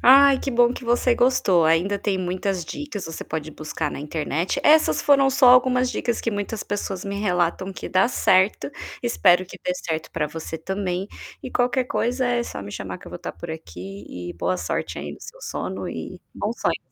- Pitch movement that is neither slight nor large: No, wide, 7.1 semitones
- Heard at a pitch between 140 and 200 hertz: Yes, high, 190 Hz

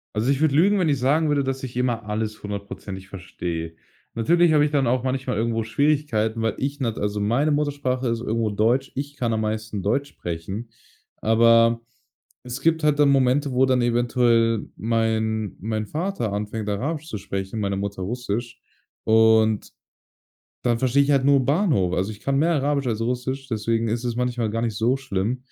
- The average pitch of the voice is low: Yes, low, 120 Hz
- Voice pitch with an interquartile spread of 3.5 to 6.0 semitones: Yes, average, 3.9 semitones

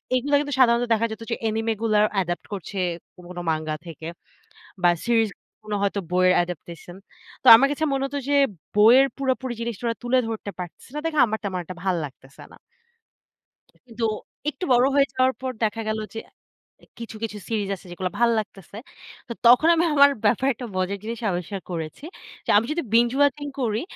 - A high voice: Yes, high, 225 Hz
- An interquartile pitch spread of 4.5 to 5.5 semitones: Yes, average, 5.2 semitones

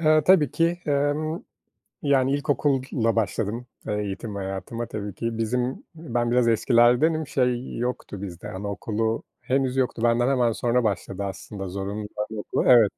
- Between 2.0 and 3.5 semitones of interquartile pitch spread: No, average, 4.3 semitones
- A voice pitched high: No, low, 120 Hz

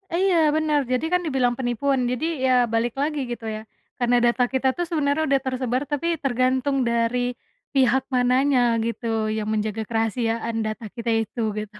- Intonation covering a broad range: No, average, 2.8 semitones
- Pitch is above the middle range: Yes, very high, 250 Hz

